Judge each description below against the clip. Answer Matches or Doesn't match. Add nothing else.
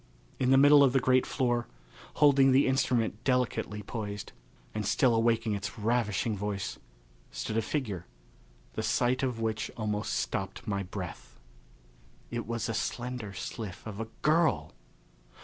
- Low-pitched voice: Matches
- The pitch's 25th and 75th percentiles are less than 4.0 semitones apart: Matches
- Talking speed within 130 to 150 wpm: Matches